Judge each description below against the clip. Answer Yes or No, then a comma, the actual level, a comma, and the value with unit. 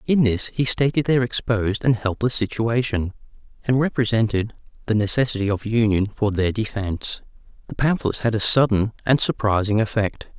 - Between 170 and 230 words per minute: No, average, 150 wpm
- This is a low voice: Yes, low, 115 Hz